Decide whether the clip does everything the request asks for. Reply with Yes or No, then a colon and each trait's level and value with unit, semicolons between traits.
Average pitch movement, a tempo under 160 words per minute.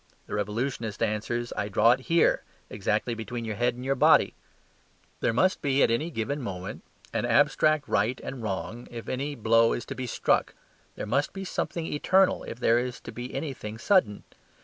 No: average, 3.8 semitones; average, 180 wpm